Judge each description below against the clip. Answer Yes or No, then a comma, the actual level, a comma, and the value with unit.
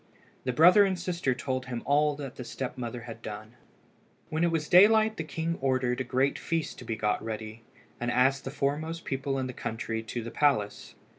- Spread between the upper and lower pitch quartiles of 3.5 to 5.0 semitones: Yes, average, 4.7 semitones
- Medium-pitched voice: No, low, 130 Hz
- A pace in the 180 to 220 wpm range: Yes, fast, 205 wpm